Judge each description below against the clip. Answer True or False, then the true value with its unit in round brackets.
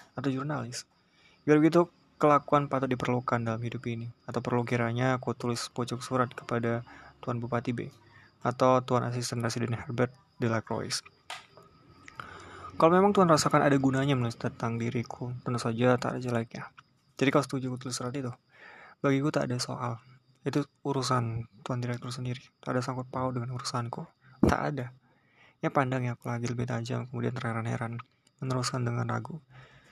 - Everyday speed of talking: False (155 wpm)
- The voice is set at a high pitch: False (125 Hz)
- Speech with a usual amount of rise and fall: False (1.8 semitones)